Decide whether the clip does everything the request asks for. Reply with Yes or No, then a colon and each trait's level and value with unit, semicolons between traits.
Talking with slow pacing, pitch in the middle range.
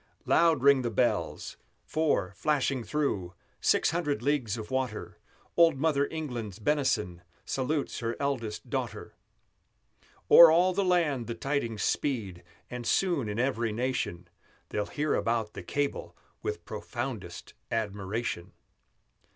No: slow, 125 wpm; low, 130 Hz